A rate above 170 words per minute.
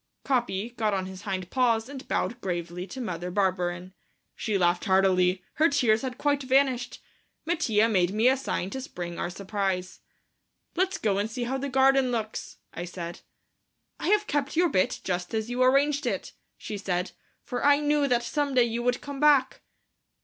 Yes: average, 180 wpm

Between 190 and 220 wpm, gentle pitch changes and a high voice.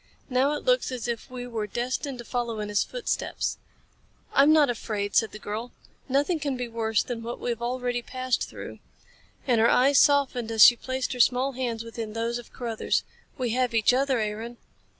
Yes: average, 195 wpm; narrow, 2.2 semitones; high, 245 Hz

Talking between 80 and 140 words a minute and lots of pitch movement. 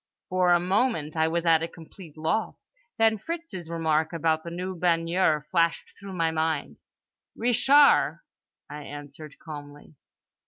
No: slow, 135 wpm; average, 3.0 semitones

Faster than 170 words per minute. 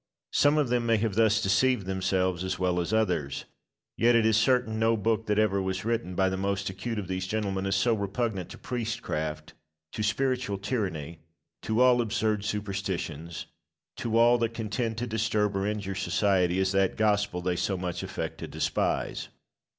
Yes: average, 180 wpm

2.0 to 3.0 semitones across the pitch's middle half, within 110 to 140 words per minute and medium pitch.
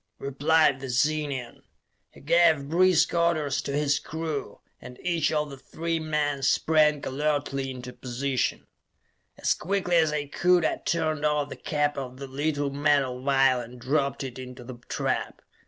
No: average, 2.7 semitones; average, 155 wpm; medium, 145 Hz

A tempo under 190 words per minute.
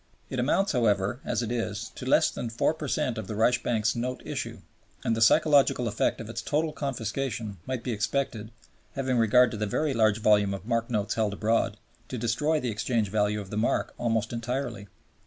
No: average, 195 wpm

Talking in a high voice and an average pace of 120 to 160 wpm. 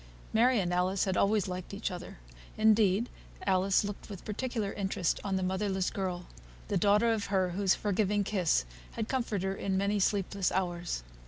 No: high, 195 Hz; average, 175 wpm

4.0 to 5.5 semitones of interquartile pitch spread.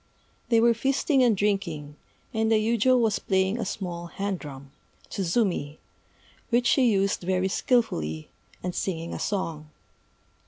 Yes: average, 5.1 semitones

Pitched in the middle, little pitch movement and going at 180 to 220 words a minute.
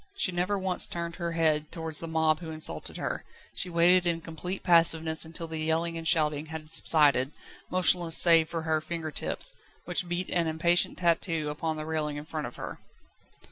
Yes: medium, 165 Hz; narrow, 1.6 semitones; average, 185 wpm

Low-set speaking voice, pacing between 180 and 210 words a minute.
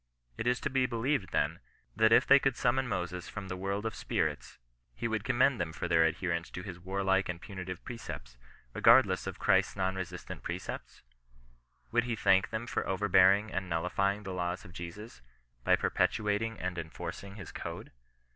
Yes: very low, 95 Hz; average, 185 wpm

